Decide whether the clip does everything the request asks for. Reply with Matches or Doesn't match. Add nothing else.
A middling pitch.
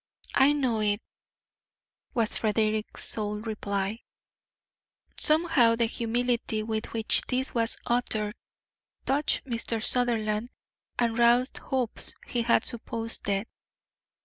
Doesn't match